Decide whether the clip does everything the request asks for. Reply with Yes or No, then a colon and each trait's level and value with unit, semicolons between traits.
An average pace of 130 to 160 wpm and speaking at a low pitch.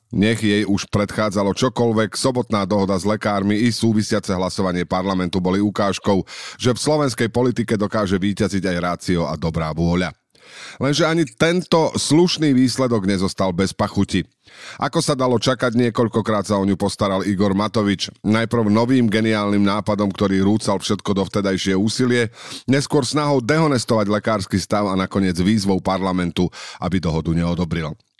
Yes: average, 145 wpm; low, 105 Hz